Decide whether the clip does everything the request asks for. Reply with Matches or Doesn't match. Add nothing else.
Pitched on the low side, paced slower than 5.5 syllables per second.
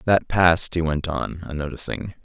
Matches